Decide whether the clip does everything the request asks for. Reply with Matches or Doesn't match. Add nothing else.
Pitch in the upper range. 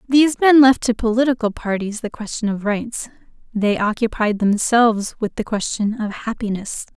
Matches